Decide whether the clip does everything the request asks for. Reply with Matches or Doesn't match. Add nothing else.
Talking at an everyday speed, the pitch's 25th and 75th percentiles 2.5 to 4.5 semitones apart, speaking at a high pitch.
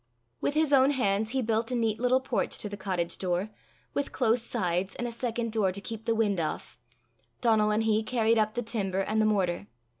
Doesn't match